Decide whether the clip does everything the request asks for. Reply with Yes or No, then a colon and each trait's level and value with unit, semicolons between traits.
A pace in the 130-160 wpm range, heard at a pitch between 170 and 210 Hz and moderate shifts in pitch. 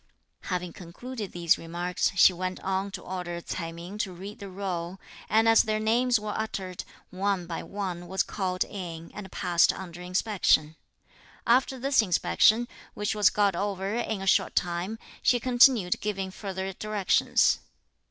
Yes: average, 155 wpm; high, 190 Hz; average, 3.1 semitones